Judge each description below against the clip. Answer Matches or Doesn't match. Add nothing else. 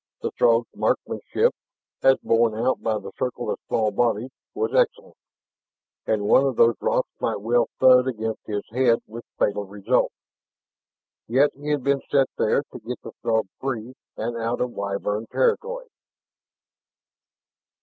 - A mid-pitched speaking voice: Doesn't match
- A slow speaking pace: Doesn't match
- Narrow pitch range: Doesn't match